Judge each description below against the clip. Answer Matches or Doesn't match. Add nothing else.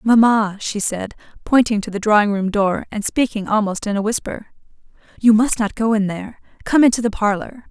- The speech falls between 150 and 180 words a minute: Doesn't match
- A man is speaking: Doesn't match